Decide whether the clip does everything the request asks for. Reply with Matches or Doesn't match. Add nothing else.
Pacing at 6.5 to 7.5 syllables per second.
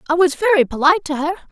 Doesn't match